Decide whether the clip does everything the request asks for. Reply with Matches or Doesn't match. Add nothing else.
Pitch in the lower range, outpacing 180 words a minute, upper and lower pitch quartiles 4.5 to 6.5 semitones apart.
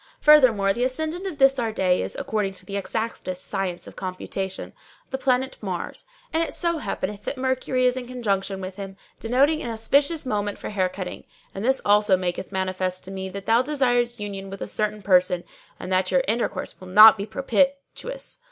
Doesn't match